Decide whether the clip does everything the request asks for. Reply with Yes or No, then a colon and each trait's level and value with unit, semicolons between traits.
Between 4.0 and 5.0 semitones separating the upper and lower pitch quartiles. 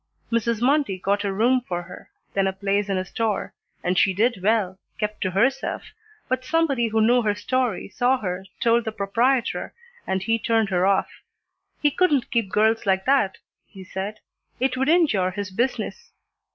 Yes: average, 4.5 semitones